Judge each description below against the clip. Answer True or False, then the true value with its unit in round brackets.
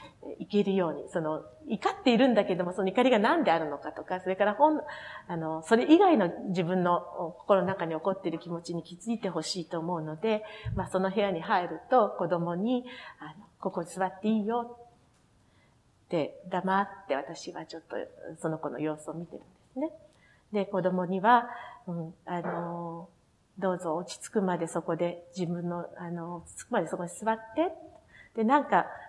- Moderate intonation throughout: True (4.8 semitones)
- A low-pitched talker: False (185 Hz)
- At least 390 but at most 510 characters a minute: False (330 characters per minute)